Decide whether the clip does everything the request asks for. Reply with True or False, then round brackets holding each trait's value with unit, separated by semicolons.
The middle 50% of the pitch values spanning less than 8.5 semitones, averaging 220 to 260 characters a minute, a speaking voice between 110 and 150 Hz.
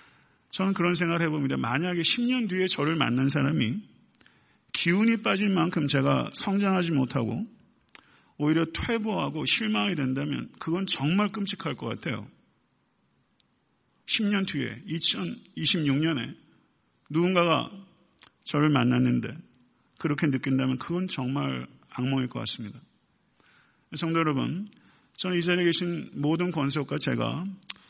False (5.3 semitones; 255 characters per minute; 165 Hz)